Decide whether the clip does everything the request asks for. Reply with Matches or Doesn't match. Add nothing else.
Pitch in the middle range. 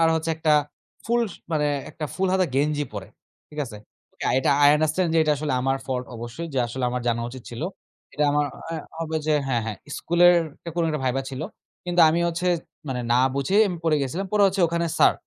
Matches